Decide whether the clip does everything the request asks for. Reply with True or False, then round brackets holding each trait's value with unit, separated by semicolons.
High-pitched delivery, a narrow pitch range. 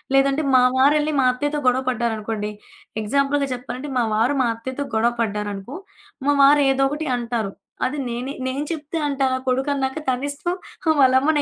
False (265 Hz; 3.1 semitones)